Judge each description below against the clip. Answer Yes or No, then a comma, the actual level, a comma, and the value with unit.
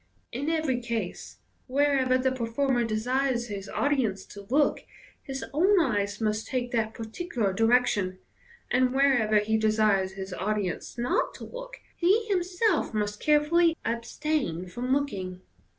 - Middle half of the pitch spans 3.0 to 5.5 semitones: Yes, average, 5.1 semitones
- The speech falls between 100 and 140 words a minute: Yes, slow, 135 wpm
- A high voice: Yes, high, 245 Hz